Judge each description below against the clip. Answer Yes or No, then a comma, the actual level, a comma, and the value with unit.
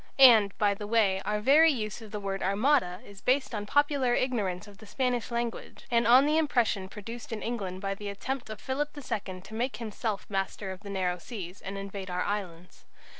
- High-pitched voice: Yes, high, 210 Hz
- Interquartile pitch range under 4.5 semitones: Yes, average, 3.7 semitones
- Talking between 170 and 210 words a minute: Yes, fast, 205 wpm